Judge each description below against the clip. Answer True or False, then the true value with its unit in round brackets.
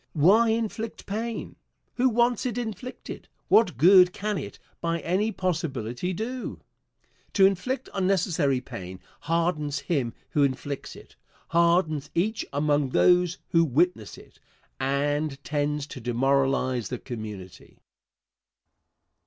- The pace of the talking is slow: True (115 wpm)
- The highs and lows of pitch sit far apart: True (6.3 semitones)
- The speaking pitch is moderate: True (165 Hz)